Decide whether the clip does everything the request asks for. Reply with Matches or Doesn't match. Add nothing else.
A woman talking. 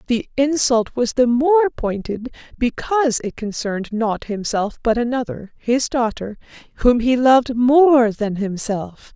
Matches